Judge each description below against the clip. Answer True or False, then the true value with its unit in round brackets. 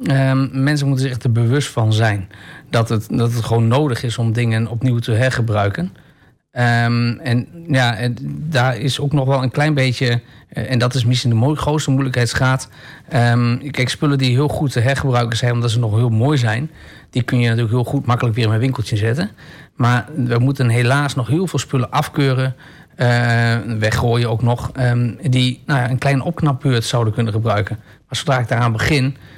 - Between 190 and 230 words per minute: True (195 wpm)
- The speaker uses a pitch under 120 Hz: False (125 Hz)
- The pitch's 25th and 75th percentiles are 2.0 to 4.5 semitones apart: True (2.6 semitones)